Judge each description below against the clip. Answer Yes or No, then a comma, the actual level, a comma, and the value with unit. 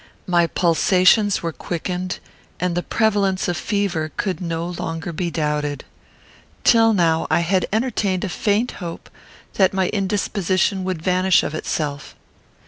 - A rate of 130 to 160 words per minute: Yes, slow, 135 wpm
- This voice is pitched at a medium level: Yes, medium, 180 Hz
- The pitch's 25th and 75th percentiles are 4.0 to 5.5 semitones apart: No, average, 2.9 semitones